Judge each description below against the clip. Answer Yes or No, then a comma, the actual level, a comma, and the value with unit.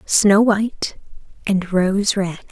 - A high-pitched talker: Yes, high, 200 Hz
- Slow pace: Yes, slow, 120 wpm